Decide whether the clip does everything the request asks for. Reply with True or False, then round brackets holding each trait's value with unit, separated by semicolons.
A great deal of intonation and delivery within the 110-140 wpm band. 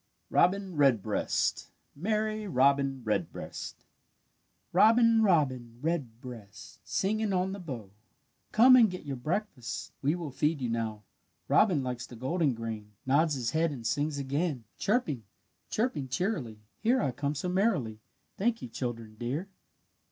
True (7.6 semitones; 135 wpm)